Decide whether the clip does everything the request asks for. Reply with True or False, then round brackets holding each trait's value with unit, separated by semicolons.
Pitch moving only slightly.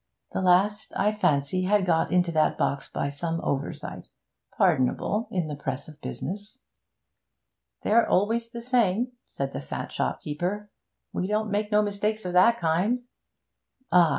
False (4.7 semitones)